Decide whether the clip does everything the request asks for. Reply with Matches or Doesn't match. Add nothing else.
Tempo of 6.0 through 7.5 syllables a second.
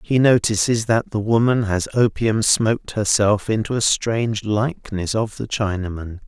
Doesn't match